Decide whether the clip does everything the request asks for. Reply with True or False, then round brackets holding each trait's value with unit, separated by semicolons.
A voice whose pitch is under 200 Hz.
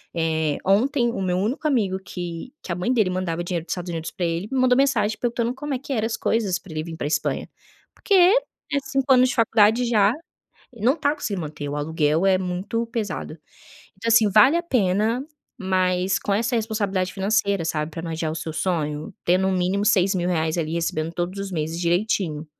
True (190 Hz)